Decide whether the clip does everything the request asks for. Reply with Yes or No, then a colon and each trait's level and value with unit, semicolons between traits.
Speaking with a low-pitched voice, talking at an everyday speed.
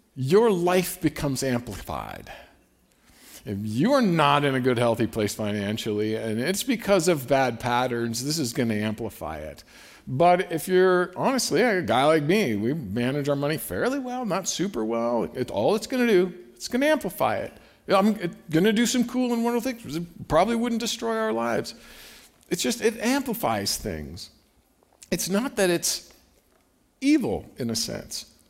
No: medium, 160 Hz; average, 170 wpm